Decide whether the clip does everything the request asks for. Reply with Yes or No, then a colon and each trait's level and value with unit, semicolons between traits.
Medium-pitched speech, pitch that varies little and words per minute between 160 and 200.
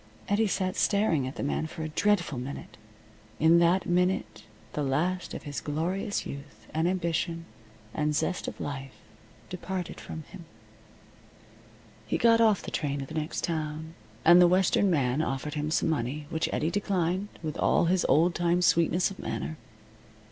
No: medium, 165 Hz; average, 3.4 semitones; average, 165 wpm